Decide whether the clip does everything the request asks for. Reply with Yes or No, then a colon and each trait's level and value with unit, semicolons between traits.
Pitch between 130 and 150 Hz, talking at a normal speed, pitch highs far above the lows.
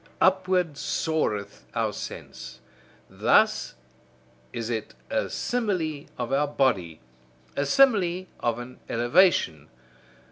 No: medium, 140 Hz; slow, 100 wpm; wide, 7.6 semitones